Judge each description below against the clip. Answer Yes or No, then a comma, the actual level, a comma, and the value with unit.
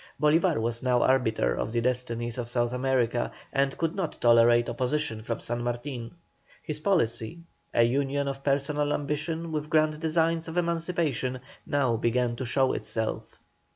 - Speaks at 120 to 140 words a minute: No, average, 155 wpm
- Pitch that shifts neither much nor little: Yes, average, 4.4 semitones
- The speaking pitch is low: Yes, low, 130 Hz